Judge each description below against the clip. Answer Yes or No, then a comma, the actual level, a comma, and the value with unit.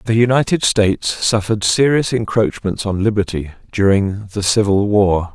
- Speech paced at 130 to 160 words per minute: Yes, slow, 135 wpm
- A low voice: Yes, low, 105 Hz